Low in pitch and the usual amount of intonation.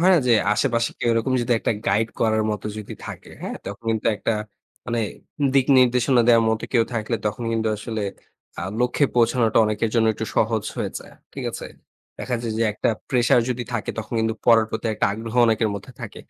No: low, 115 Hz; narrow, 1.6 semitones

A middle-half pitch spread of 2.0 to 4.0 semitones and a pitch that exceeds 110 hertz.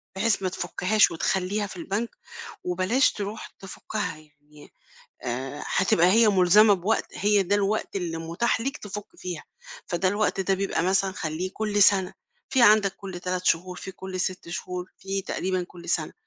Yes: narrow, 2.6 semitones; high, 190 Hz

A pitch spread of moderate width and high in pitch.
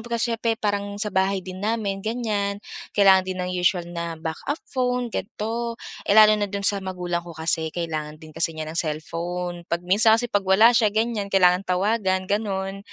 Yes: average, 3.5 semitones; high, 195 Hz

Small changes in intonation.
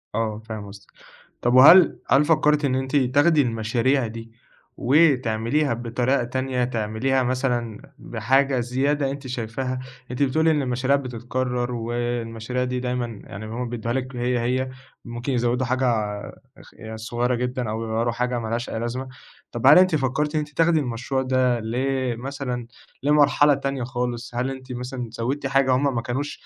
Yes: narrow, 2.2 semitones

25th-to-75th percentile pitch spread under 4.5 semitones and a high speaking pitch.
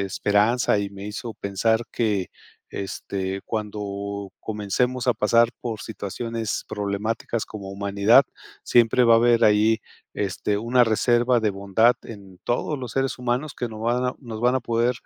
No: average, 3.0 semitones; low, 110 Hz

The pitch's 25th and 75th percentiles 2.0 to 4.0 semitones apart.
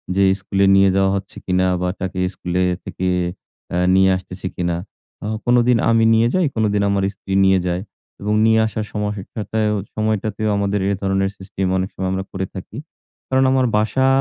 Yes: narrow, 2.4 semitones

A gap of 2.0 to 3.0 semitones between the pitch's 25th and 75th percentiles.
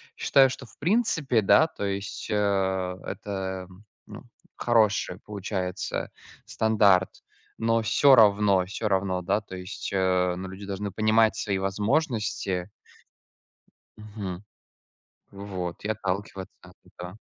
Yes: narrow, 2.6 semitones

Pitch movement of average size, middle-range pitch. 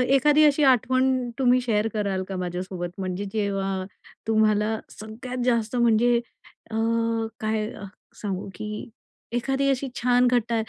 No: average, 3.5 semitones; high, 220 Hz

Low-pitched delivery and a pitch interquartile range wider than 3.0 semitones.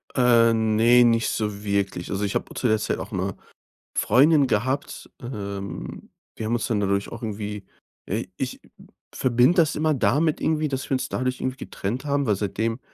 Yes: low, 115 Hz; average, 4.1 semitones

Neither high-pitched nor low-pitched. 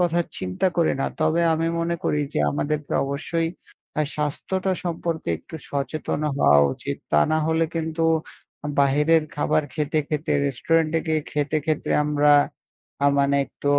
Yes: medium, 155 Hz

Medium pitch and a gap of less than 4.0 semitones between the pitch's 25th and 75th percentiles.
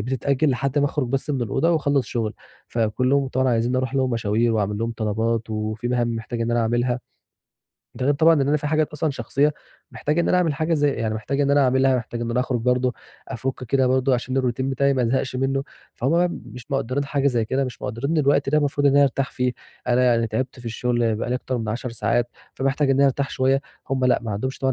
No: low, 130 Hz; average, 2.8 semitones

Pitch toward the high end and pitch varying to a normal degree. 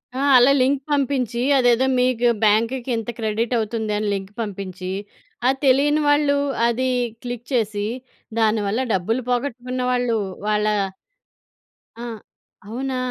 Yes: high, 240 Hz; average, 3.1 semitones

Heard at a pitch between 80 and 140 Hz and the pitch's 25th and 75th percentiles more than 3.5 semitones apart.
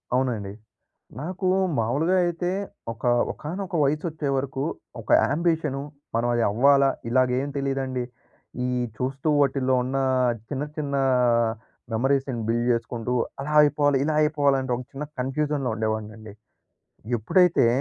No: low, 135 Hz; average, 3.2 semitones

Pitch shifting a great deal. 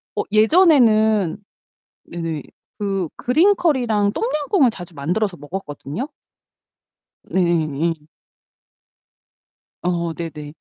Yes: wide, 6.5 semitones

